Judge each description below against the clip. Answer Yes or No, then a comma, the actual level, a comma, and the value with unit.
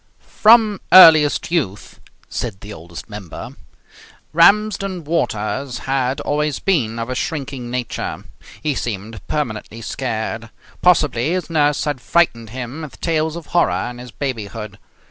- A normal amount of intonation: No, wide, 6.1 semitones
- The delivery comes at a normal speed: No, slow, 130 wpm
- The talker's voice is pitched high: No, low, 135 Hz